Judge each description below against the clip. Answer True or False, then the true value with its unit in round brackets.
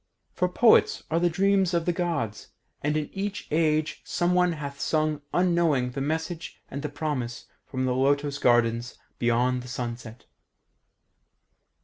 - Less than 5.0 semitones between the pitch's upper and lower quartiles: False (5.3 semitones)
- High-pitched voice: False (150 Hz)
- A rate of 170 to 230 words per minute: False (140 wpm)